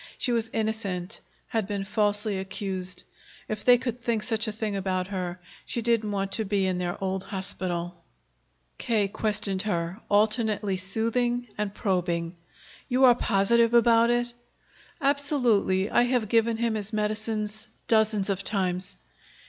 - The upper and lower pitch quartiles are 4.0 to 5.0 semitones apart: No, average, 3.1 semitones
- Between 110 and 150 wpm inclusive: Yes, average, 145 wpm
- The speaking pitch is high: Yes, high, 210 Hz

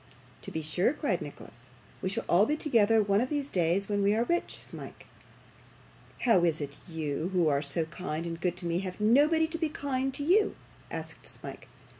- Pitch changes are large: Yes, wide, 8.1 semitones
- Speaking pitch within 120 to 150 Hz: No, high, 200 Hz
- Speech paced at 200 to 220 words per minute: Yes, fast, 205 wpm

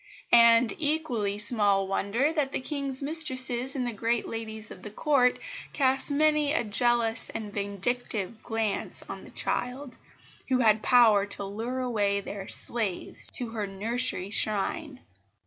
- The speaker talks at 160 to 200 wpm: No, average, 145 wpm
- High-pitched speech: Yes, high, 235 Hz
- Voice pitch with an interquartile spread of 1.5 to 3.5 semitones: No, average, 3.9 semitones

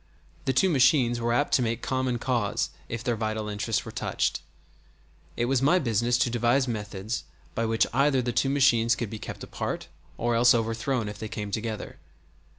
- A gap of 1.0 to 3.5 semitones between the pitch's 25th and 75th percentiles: Yes, narrow, 2.6 semitones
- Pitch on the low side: Yes, low, 120 Hz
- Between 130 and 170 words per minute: No, average, 185 wpm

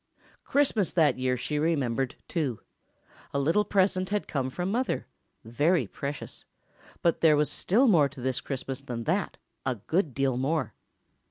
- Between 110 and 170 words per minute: Yes, average, 140 wpm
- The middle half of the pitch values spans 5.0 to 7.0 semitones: Yes, wide, 5.4 semitones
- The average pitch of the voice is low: No, medium, 145 Hz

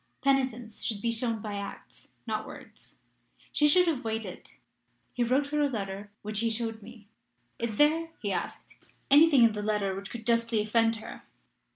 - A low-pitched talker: No, high, 230 Hz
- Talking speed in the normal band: Yes, average, 175 wpm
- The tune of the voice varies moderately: Yes, average, 3.4 semitones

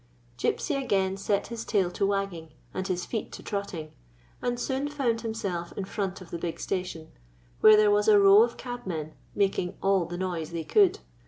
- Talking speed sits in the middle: Yes, average, 190 wpm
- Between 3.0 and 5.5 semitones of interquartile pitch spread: Yes, average, 3.9 semitones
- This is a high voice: Yes, high, 195 Hz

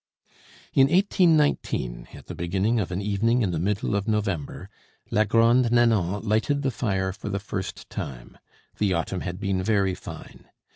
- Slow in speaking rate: No, average, 160 wpm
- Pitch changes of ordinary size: Yes, average, 3.7 semitones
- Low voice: Yes, low, 100 Hz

